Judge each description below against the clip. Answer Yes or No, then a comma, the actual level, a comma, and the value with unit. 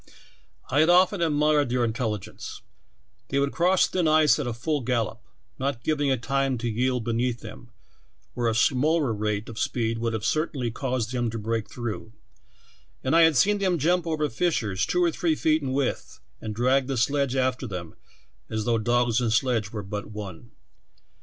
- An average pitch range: Yes, average, 4.7 semitones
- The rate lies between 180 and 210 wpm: Yes, average, 185 wpm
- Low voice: Yes, low, 125 Hz